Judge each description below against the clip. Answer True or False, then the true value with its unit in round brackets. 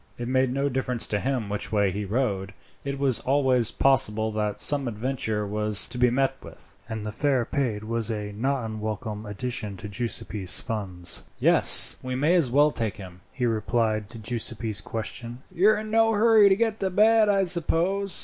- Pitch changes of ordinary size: True (4.7 semitones)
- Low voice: True (120 Hz)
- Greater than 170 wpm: True (190 wpm)